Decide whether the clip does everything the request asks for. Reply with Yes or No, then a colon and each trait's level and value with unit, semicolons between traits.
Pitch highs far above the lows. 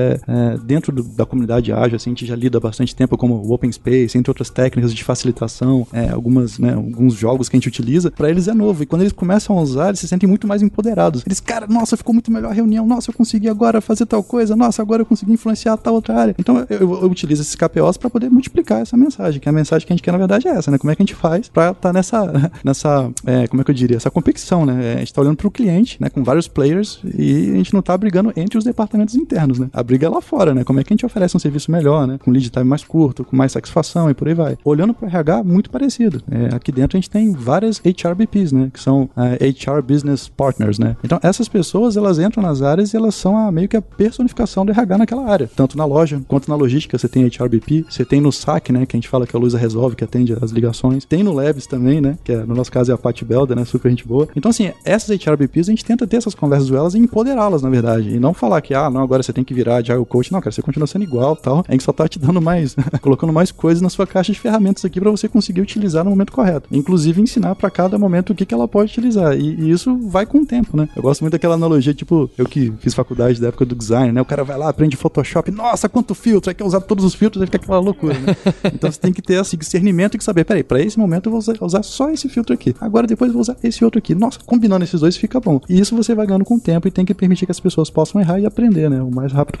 Yes: wide, 7.8 semitones